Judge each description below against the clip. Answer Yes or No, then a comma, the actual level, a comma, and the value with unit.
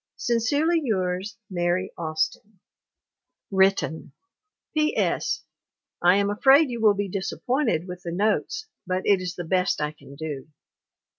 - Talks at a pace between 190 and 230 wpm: No, slow, 135 wpm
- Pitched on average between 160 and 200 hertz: Yes, high, 190 Hz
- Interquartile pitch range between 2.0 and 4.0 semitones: No, average, 4.5 semitones